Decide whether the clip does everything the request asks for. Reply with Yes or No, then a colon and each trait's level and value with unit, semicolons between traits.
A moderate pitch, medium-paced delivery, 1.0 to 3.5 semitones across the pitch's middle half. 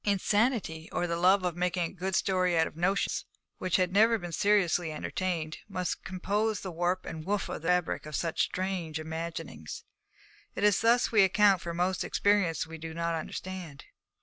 Yes: medium, 180 Hz; average, 180 wpm; average, 2.9 semitones